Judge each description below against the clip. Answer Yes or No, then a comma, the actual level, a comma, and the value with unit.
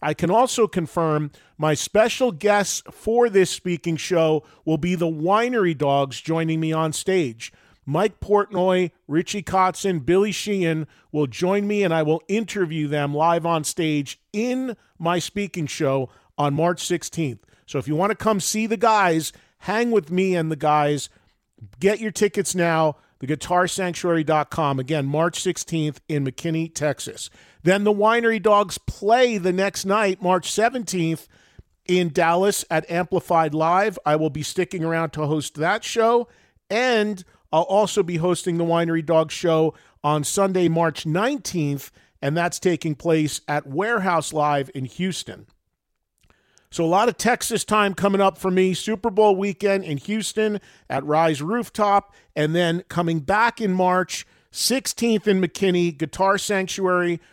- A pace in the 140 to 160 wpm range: Yes, average, 150 wpm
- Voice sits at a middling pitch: Yes, medium, 175 Hz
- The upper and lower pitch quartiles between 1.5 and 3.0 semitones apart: No, average, 4.3 semitones